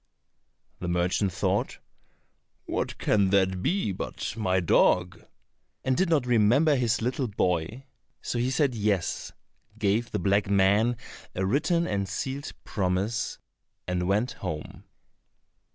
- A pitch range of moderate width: Yes, average, 4.8 semitones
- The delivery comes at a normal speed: No, slow, 125 wpm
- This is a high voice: No, low, 105 Hz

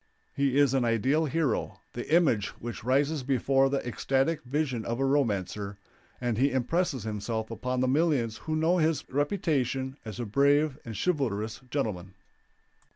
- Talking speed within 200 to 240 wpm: No, average, 155 wpm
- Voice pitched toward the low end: Yes, low, 130 Hz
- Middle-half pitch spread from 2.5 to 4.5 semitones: Yes, average, 4.0 semitones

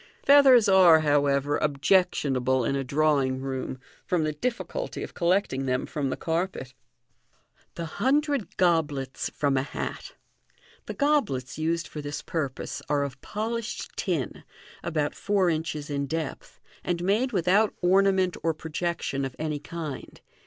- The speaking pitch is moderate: Yes, medium, 160 Hz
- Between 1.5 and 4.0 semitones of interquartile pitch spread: No, average, 5.3 semitones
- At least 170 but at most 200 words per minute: No, average, 145 wpm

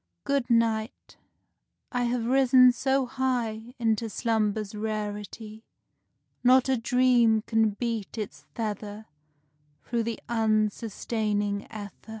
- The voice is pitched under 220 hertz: No, high, 225 Hz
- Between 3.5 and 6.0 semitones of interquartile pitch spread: No, narrow, 2.4 semitones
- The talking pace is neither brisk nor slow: No, slow, 105 wpm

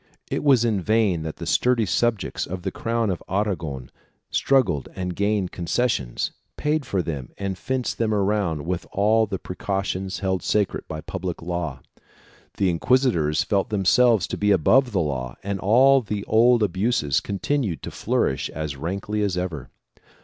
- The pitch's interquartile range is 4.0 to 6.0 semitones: Yes, average, 4.4 semitones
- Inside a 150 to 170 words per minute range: Yes, average, 160 wpm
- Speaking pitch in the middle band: No, low, 100 Hz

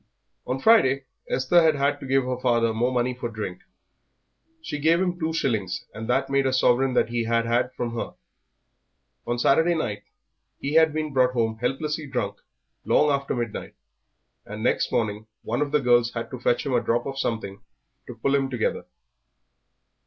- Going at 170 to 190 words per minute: Yes, average, 180 wpm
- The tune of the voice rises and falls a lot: No, average, 3.1 semitones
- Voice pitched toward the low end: Yes, low, 125 Hz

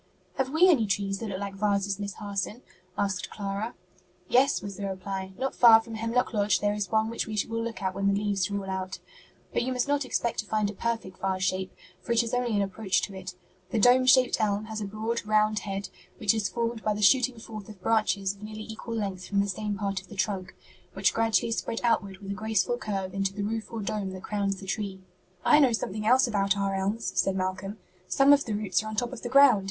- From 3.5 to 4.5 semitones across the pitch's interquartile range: No, narrow, 2.6 semitones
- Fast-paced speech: Yes, fast, 240 wpm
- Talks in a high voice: Yes, high, 210 Hz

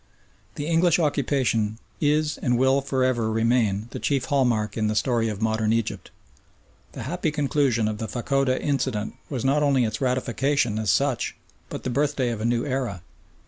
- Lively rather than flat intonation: No, average, 4.0 semitones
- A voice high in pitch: No, low, 125 Hz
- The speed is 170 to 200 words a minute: Yes, average, 175 wpm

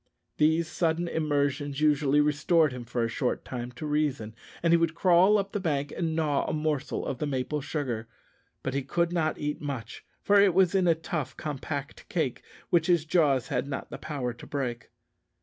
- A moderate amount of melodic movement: Yes, average, 3.4 semitones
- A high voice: No, medium, 150 Hz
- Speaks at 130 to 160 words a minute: No, average, 190 wpm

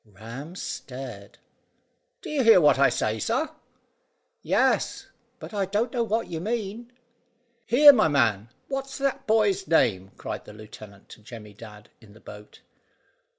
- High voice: No, medium, 150 Hz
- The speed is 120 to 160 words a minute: Yes, average, 145 wpm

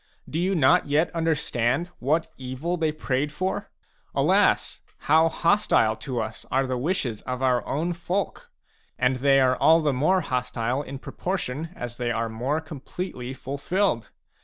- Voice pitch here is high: No, medium, 140 Hz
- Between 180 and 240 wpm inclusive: No, average, 155 wpm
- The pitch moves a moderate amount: Yes, average, 4.5 semitones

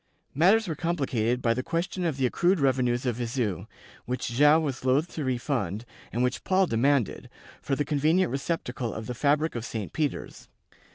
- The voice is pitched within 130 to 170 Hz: Yes, low, 135 Hz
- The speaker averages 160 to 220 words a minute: Yes, average, 175 wpm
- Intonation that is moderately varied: Yes, average, 4.5 semitones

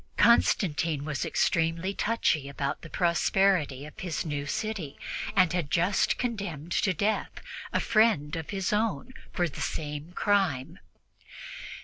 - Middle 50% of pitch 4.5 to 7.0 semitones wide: Yes, average, 5.1 semitones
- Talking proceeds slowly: Yes, slow, 130 wpm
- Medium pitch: Yes, medium, 170 Hz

